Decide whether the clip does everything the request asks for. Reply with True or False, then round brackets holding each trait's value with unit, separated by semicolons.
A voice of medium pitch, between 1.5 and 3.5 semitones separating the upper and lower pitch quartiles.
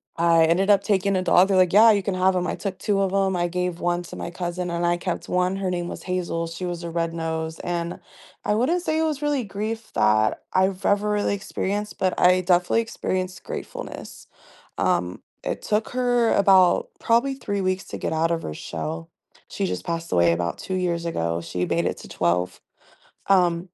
True (180 Hz; 2.9 semitones)